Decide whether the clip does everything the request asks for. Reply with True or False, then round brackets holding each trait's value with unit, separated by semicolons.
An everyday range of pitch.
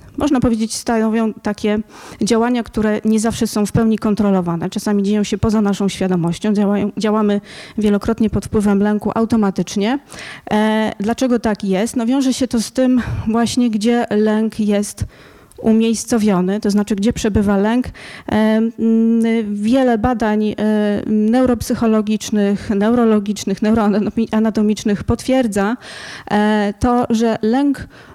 False (1.7 semitones)